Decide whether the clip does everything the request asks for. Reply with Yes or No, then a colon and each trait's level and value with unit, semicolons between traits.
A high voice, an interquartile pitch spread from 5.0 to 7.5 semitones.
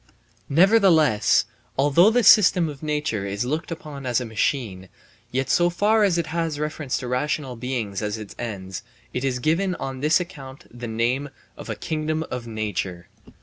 No: low, 135 Hz; wide, 5.6 semitones